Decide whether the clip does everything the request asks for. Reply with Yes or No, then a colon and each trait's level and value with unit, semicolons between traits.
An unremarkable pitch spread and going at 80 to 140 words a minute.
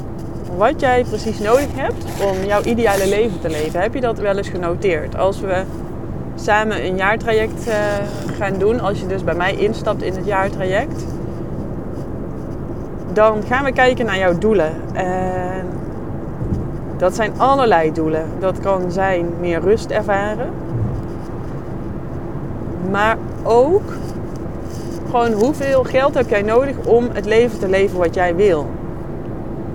Yes: average, 4.5 semitones; slow, 135 wpm